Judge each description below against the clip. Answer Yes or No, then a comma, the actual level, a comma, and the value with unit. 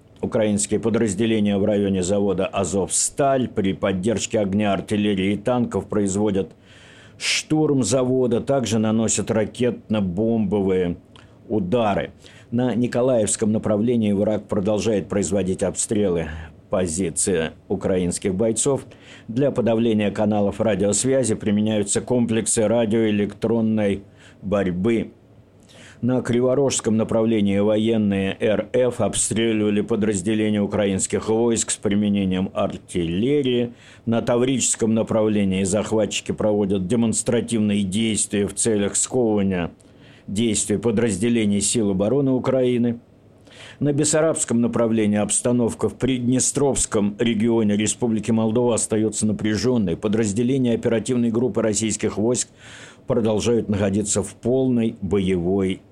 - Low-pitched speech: Yes, low, 110 Hz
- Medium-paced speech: No, slow, 90 wpm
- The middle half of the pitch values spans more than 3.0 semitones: No, narrow, 2.6 semitones